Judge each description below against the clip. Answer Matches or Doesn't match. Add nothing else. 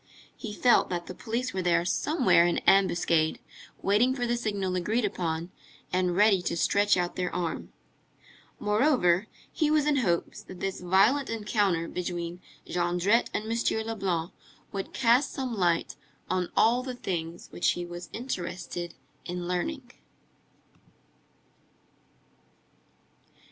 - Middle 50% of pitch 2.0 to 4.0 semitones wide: Doesn't match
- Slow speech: Matches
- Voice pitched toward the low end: Doesn't match